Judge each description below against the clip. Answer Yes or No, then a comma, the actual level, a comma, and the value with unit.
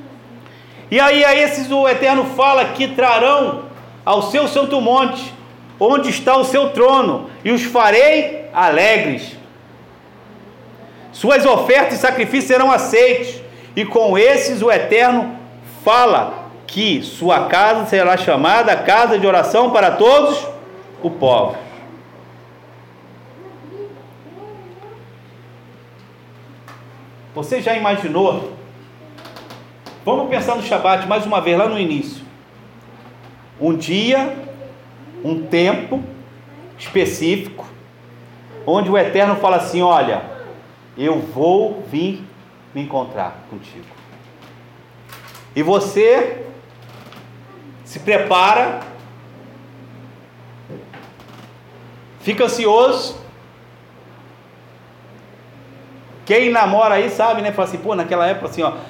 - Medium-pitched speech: No, high, 195 Hz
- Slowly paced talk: Yes, slow, 95 wpm